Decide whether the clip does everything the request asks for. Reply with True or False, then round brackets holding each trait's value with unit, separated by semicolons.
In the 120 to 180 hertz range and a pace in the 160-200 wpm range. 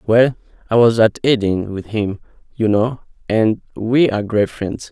False (110 Hz; 170 wpm)